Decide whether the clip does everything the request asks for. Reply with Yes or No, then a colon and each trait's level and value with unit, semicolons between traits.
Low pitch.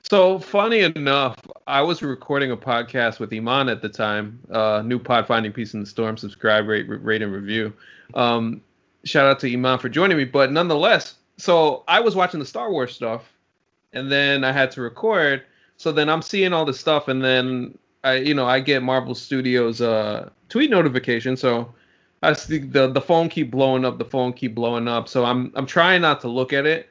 Yes: low, 130 Hz